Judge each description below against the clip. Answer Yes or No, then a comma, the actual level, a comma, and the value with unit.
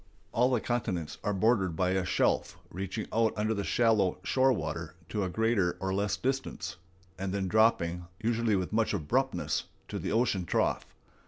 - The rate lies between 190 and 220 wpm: No, average, 170 wpm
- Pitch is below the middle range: Yes, low, 105 Hz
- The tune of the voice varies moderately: Yes, average, 3.6 semitones